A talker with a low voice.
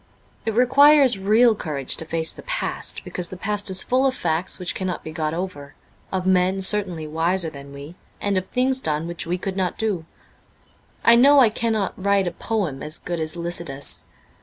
No: medium, 185 Hz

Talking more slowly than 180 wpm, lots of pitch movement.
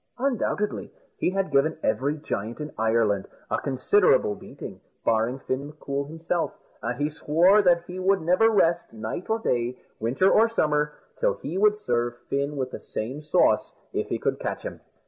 Yes: average, 170 wpm; wide, 6.6 semitones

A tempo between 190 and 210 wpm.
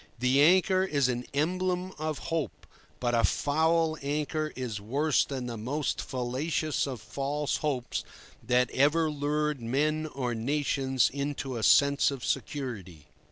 No: average, 140 wpm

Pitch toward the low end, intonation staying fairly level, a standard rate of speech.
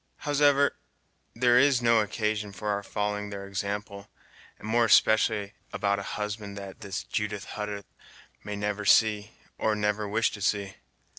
Yes: low, 105 Hz; narrow, 1.5 semitones; average, 150 wpm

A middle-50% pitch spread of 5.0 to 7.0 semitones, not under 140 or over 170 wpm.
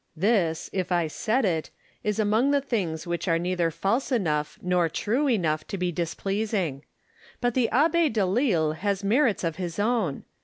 Yes: wide, 5.4 semitones; average, 165 wpm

